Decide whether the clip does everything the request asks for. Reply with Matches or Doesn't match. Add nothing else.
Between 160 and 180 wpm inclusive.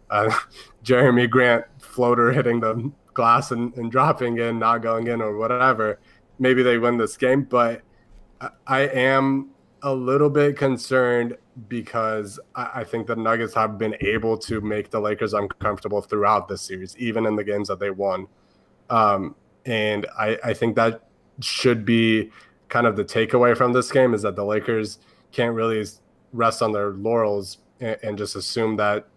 Matches